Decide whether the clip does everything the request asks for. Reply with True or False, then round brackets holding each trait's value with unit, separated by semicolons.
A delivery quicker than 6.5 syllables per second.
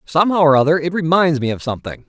True (7.1 syllables/s)